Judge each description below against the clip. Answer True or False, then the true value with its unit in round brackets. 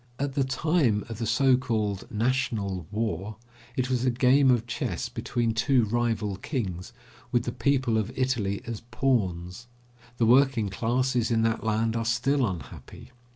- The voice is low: True (115 Hz)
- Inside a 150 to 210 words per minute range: True (155 wpm)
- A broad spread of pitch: False (3.2 semitones)